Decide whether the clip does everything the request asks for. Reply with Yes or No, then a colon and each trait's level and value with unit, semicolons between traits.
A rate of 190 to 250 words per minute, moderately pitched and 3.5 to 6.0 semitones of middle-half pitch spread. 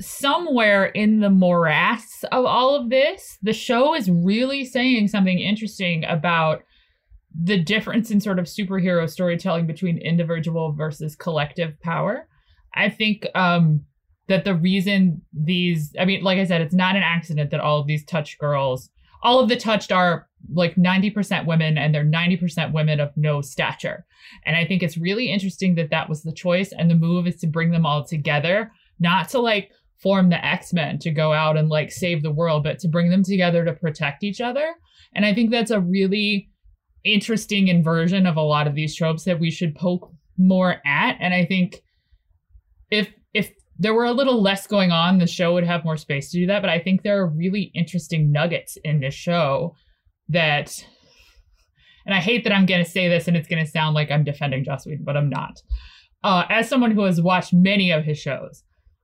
Yes: average, 195 wpm; medium, 175 Hz; average, 4.0 semitones